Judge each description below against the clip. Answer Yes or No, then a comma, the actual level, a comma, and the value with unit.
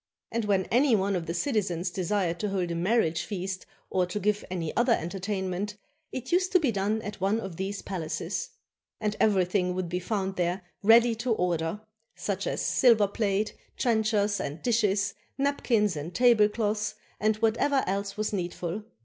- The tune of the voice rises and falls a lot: No, average, 3.1 semitones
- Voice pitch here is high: Yes, high, 200 Hz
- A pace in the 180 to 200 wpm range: No, average, 165 wpm